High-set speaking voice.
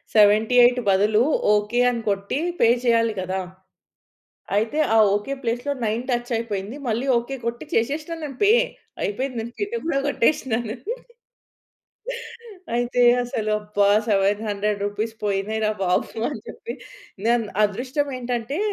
Yes: high, 230 Hz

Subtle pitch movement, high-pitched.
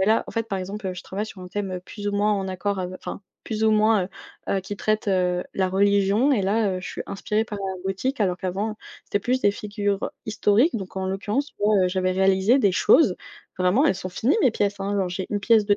Yes: narrow, 2.1 semitones; high, 200 Hz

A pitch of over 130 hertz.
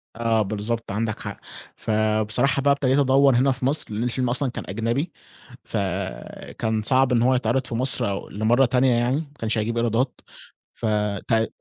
No: low, 120 Hz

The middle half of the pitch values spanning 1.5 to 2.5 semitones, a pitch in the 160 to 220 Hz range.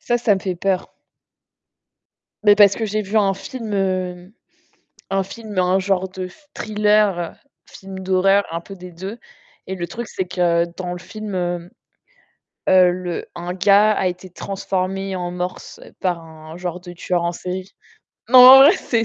Yes: narrow, 2.2 semitones; high, 190 Hz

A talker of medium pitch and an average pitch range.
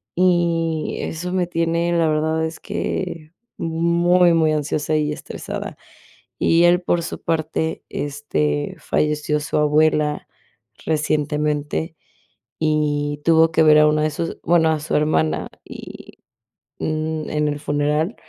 No: medium, 155 Hz; narrow, 1.7 semitones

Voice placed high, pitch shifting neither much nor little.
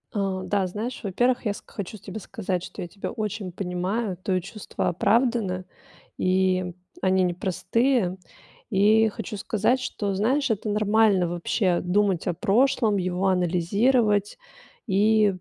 Yes: high, 200 Hz; average, 3.0 semitones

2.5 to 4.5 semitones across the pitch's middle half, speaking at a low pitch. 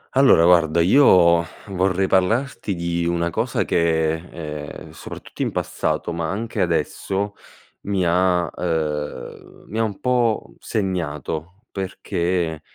Yes: average, 2.8 semitones; very low, 90 Hz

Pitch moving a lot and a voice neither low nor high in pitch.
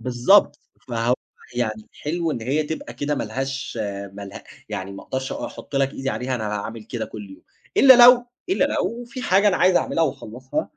No: wide, 6.6 semitones; low, 130 Hz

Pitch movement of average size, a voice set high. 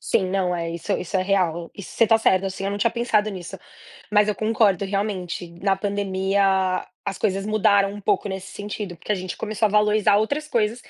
No: narrow, 1.9 semitones; high, 200 Hz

